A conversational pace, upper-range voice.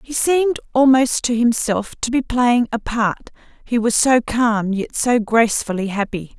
Yes: average, 170 wpm; high, 235 Hz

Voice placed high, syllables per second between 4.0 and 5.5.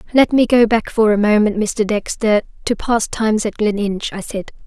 Yes: high, 215 Hz; 5.0 syllables/s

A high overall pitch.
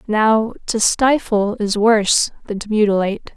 Yes: high, 215 Hz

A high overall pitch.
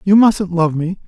No: medium, 180 Hz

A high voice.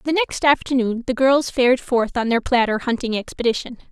Yes: very high, 250 Hz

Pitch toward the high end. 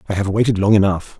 No: low, 100 Hz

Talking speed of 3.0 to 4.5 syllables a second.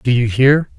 Yes: 4.4 syllables/s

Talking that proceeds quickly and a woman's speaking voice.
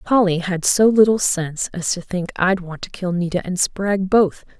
Yes: fast, 210 wpm; female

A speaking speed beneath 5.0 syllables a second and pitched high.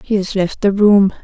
Yes: 4.6 syllables/s; high, 200 Hz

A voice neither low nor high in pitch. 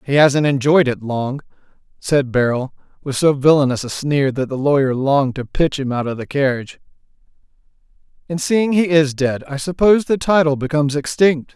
Yes: medium, 145 Hz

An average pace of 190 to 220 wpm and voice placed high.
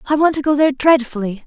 No: fast, 245 wpm; very high, 275 Hz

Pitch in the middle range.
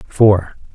No: low, 100 Hz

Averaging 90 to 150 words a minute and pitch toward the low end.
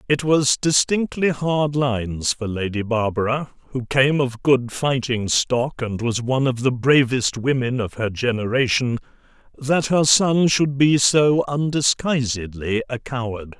Yes: average, 145 wpm; low, 130 Hz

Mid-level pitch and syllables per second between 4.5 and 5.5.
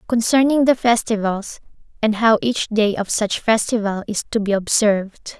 No: high, 220 Hz; 4.7 syllables/s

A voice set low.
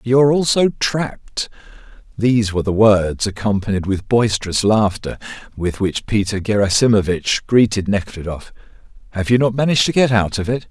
Yes: low, 105 Hz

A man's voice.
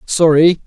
Yes: male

